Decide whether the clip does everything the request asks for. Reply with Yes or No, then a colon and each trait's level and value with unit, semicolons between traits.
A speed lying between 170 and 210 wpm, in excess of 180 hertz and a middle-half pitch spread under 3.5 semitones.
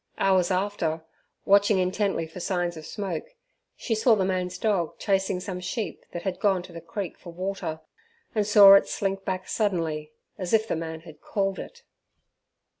Yes: average, 175 wpm; high, 190 Hz; average, 2.7 semitones